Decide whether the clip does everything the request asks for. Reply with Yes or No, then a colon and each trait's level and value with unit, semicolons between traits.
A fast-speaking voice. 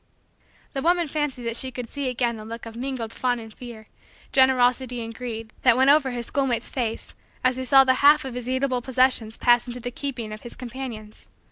Yes: fast, 210 wpm